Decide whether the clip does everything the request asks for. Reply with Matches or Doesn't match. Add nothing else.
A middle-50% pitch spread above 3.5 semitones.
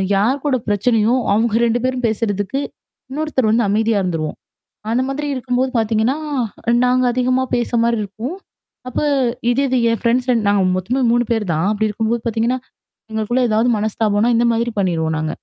Doesn't match